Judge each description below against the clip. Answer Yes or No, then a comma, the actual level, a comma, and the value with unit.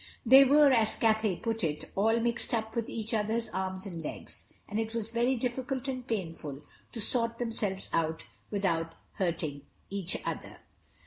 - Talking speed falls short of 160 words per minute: No, average, 165 wpm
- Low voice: No, high, 220 Hz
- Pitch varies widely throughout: No, average, 3.8 semitones